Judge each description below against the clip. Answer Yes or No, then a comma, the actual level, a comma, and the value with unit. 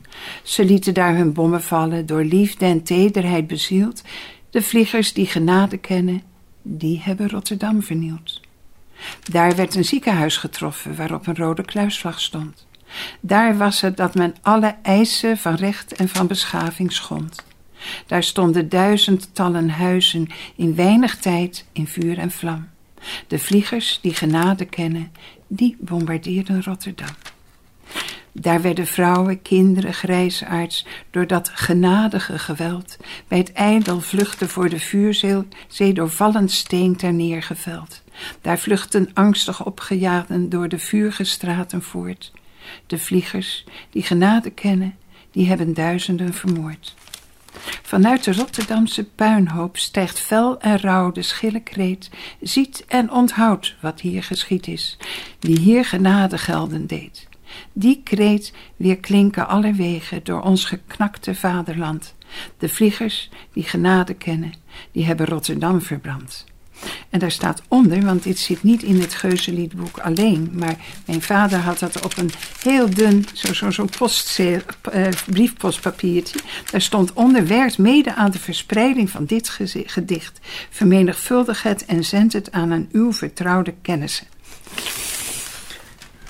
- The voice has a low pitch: No, medium, 185 Hz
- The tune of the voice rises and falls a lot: No, average, 2.8 semitones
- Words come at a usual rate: No, slow, 130 wpm